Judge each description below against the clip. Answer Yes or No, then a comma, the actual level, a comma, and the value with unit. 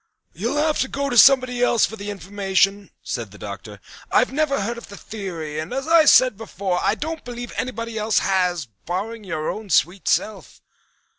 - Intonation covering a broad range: No, average, 4.9 semitones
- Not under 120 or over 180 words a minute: No, average, 190 wpm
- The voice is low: No, high, 215 Hz